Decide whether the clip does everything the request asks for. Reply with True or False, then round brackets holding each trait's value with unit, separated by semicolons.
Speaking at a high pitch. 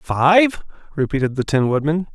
False (155 Hz)